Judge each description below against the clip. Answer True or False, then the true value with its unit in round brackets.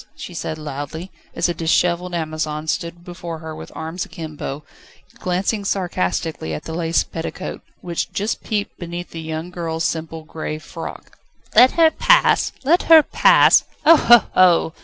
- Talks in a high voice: False (170 Hz)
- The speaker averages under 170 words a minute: True (155 wpm)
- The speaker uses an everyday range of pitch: False (2.3 semitones)